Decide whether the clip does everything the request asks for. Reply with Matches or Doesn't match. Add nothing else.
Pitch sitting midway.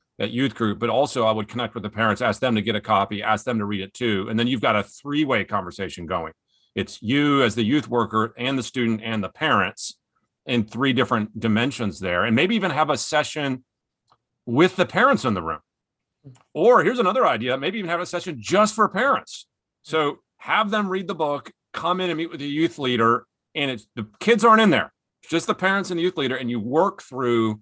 Doesn't match